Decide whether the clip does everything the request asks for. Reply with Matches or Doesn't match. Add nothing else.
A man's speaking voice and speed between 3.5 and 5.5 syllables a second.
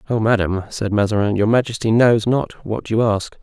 Matches